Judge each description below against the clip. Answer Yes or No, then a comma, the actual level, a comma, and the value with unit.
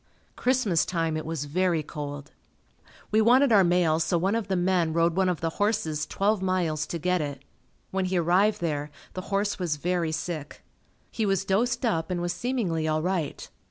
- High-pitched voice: No, medium, 175 Hz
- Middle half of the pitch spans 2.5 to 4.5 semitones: Yes, average, 3.5 semitones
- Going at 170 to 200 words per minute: Yes, average, 190 wpm